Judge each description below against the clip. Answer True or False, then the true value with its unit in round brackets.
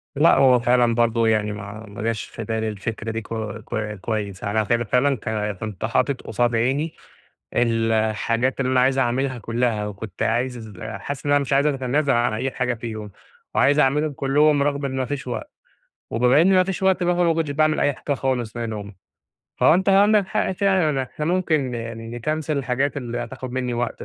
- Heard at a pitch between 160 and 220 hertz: False (125 Hz)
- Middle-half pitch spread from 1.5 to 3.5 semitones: False (4.1 semitones)